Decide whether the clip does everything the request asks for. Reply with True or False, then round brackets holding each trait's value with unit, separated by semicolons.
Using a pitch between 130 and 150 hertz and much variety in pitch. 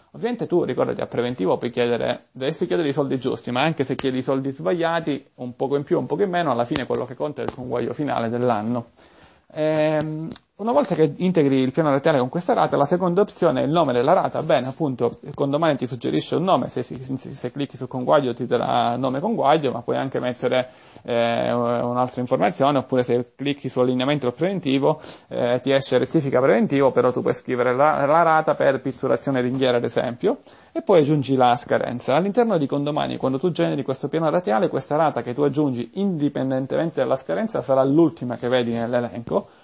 False (135 Hz; 3.8 semitones)